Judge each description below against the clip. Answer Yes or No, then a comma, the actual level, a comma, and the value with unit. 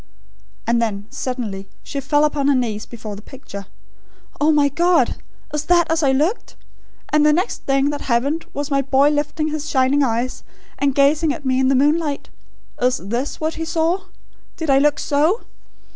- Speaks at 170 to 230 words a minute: Yes, average, 180 wpm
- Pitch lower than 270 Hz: No, very high, 285 Hz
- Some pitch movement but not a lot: Yes, average, 3.0 semitones